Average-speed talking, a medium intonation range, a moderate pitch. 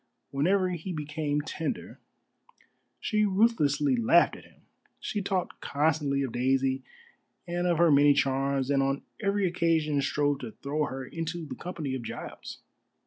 Yes: average, 145 wpm; average, 3.9 semitones; medium, 150 Hz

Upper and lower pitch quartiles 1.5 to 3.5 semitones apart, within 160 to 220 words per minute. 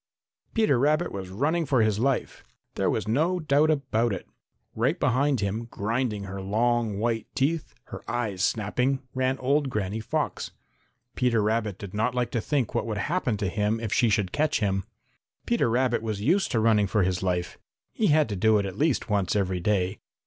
No: average, 4.6 semitones; average, 190 wpm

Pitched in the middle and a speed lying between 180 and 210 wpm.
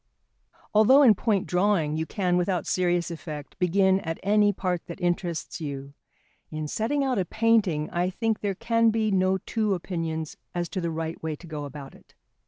Yes: medium, 180 Hz; average, 185 wpm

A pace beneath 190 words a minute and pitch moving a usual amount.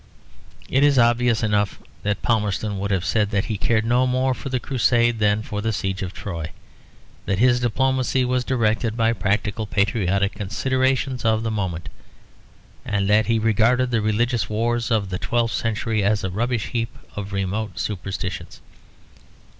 Yes: average, 160 wpm; average, 3.1 semitones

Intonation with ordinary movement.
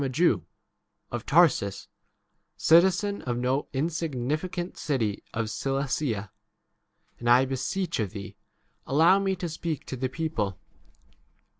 No: wide, 5.9 semitones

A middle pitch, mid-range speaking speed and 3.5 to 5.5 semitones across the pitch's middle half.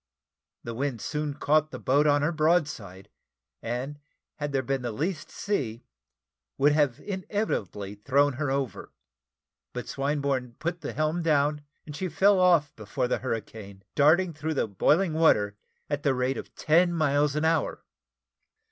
Yes: medium, 145 Hz; average, 155 wpm; average, 3.8 semitones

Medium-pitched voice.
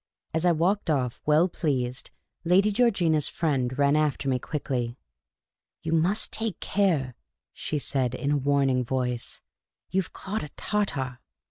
Yes: medium, 150 Hz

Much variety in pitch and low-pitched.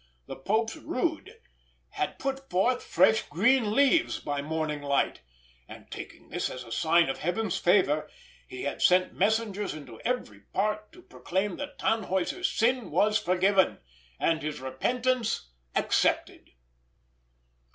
No: wide, 7.7 semitones; high, 200 Hz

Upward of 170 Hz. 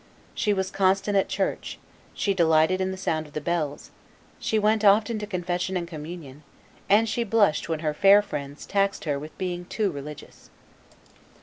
Yes: medium, 185 Hz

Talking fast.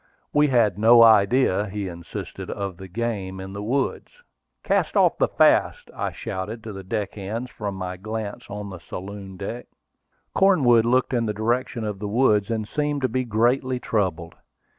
No: average, 170 wpm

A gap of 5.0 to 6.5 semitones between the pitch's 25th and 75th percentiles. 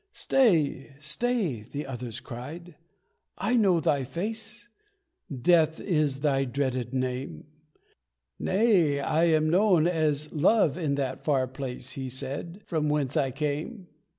No: average, 4.6 semitones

